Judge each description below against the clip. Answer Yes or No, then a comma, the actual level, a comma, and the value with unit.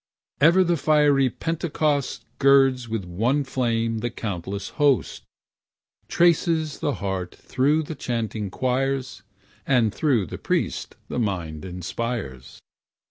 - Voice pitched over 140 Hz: No, low, 125 Hz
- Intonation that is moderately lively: No, wide, 6.0 semitones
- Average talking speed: No, slow, 110 wpm